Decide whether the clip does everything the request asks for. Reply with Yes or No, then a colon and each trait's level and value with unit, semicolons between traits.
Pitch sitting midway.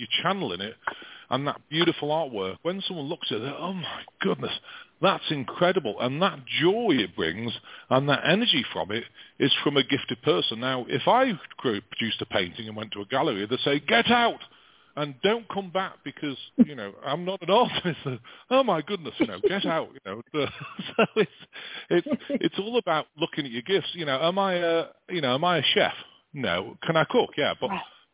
Yes: medium, 165 Hz